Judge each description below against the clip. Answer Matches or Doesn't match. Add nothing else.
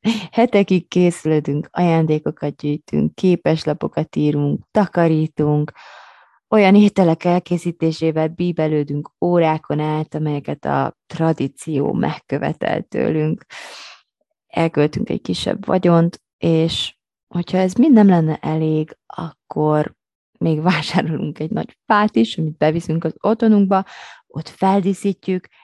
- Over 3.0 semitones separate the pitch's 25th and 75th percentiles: Matches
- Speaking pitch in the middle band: Matches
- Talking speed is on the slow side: Matches